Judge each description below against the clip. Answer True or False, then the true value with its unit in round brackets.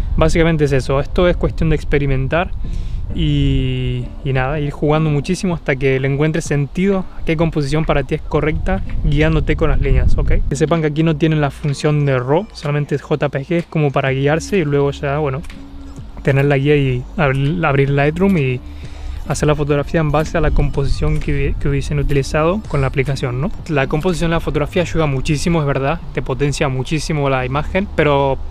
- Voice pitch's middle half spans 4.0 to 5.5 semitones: False (2.6 semitones)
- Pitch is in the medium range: True (145 Hz)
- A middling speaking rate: False (195 wpm)